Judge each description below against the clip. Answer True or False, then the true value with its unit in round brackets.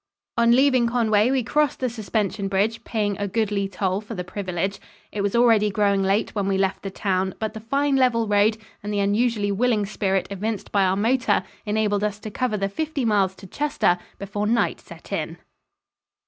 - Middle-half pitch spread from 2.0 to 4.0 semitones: True (2.8 semitones)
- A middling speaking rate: True (190 wpm)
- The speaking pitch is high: True (210 Hz)